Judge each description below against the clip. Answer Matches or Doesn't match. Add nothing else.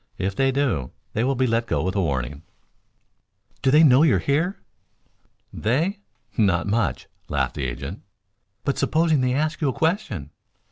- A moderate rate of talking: Matches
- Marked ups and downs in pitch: Matches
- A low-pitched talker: Matches